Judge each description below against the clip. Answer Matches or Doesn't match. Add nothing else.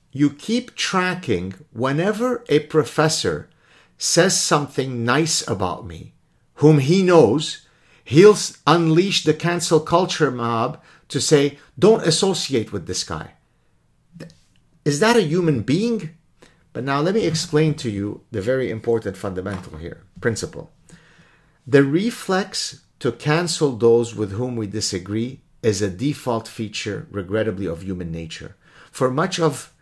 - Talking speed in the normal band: Doesn't match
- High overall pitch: Doesn't match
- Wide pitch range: Matches